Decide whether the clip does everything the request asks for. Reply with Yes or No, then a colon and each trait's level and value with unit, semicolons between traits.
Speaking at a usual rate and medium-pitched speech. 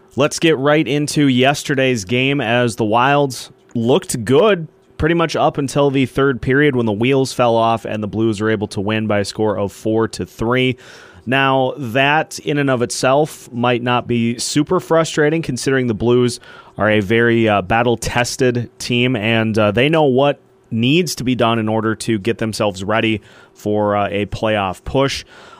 No: average, 180 wpm; low, 120 Hz